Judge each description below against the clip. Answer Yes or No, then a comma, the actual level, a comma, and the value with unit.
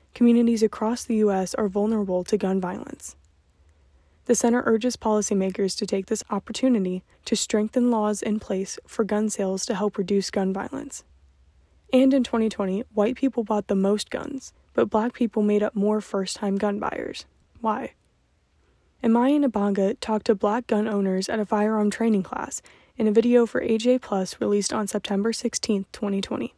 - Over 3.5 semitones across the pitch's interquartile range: No, average, 2.7 semitones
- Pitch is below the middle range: No, high, 210 Hz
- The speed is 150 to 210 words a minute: Yes, average, 165 wpm